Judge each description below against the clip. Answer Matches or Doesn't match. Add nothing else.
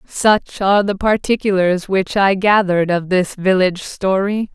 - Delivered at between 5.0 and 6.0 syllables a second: Doesn't match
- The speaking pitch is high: Matches